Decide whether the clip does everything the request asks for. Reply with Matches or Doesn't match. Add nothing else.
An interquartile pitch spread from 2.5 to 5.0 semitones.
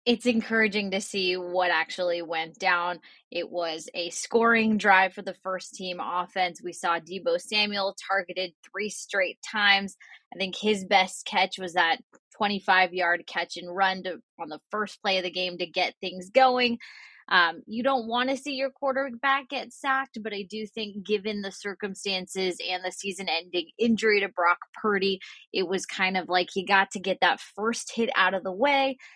Matches